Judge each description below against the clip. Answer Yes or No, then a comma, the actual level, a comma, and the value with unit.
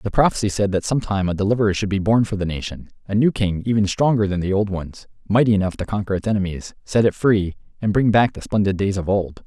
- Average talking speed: No, fast, 255 wpm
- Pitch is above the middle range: No, low, 100 Hz